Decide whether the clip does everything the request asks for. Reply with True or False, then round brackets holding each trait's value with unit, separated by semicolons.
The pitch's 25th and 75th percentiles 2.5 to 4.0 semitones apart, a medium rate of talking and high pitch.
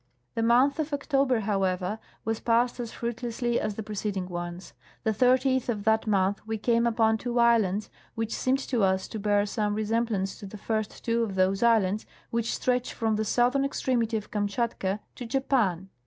True (2.8 semitones; 185 wpm; 225 Hz)